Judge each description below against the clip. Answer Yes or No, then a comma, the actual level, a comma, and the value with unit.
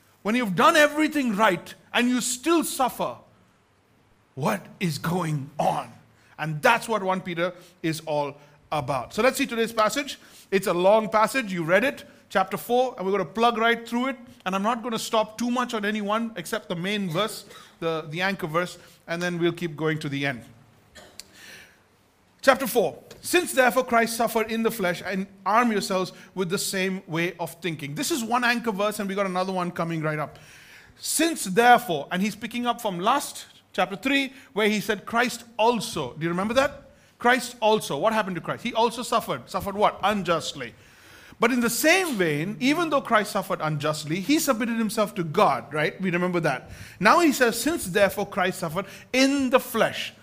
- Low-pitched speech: No, high, 205 Hz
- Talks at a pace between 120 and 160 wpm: No, average, 190 wpm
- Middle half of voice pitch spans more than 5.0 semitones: Yes, wide, 5.4 semitones